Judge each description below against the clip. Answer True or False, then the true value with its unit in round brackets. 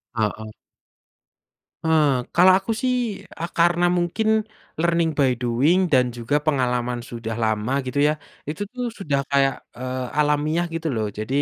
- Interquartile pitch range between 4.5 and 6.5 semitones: True (5.4 semitones)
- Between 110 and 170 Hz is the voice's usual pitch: True (140 Hz)